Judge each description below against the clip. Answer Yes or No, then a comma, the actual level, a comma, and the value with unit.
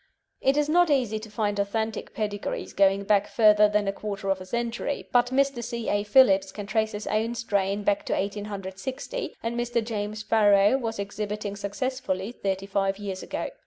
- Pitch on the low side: No, high, 210 Hz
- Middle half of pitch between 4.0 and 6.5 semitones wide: No, average, 2.9 semitones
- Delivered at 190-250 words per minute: No, average, 180 wpm